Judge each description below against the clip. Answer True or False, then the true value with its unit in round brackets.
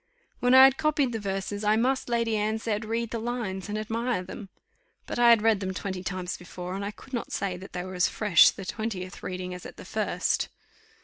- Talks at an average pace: False (230 wpm)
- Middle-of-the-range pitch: False (210 Hz)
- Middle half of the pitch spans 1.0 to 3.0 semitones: False (3.8 semitones)